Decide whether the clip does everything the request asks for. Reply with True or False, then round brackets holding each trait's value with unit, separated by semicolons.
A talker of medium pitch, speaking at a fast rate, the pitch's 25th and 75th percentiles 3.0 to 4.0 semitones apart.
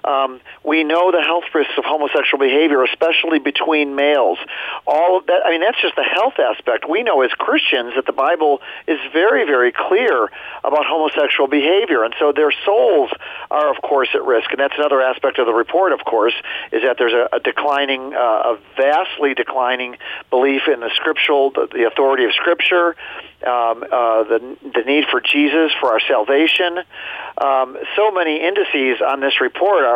False (145 Hz; 180 wpm; 3.7 semitones)